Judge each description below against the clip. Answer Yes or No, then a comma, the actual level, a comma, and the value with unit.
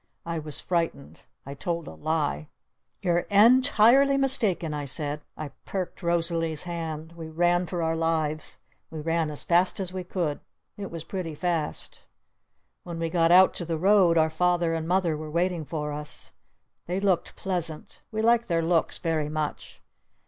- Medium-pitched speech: Yes, medium, 170 Hz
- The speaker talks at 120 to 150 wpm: No, average, 170 wpm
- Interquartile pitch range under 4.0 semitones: Yes, narrow, 2.5 semitones